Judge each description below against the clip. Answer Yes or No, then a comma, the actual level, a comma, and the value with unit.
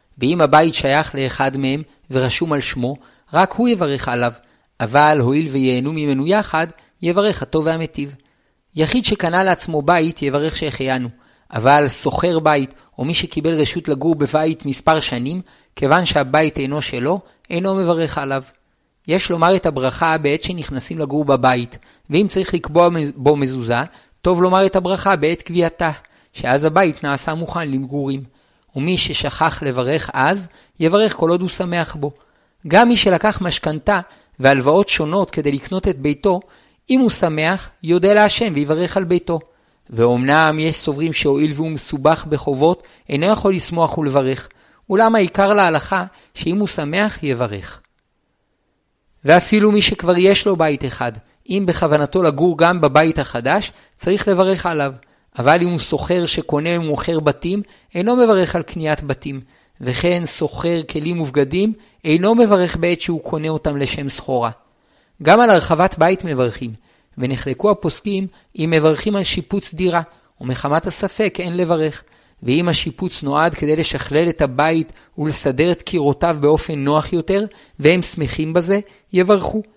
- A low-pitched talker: No, medium, 160 Hz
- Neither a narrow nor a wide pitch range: Yes, average, 4.0 semitones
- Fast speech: No, average, 140 wpm